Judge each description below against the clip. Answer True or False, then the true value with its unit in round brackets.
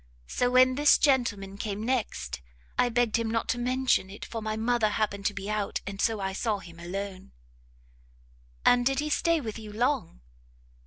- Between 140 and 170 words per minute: False (180 wpm)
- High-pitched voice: True (220 Hz)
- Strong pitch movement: False (3.7 semitones)